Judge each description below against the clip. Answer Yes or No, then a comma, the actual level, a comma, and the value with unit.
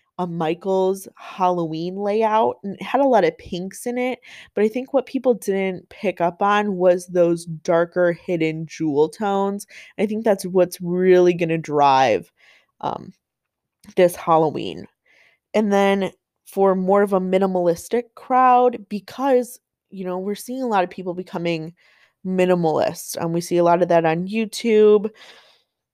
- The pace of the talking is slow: No, average, 150 wpm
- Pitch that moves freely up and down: No, average, 3.2 semitones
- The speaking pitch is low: No, high, 190 Hz